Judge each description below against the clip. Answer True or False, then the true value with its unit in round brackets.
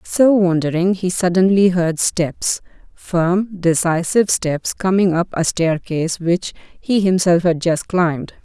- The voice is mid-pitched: True (175 Hz)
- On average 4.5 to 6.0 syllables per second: False (4.0 syllables/s)